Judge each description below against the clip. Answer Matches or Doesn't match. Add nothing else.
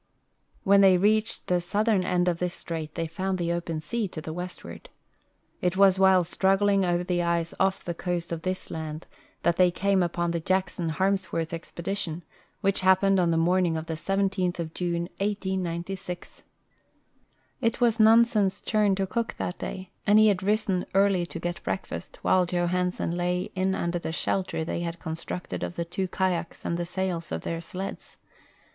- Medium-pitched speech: Matches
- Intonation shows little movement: Matches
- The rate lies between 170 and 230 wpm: Matches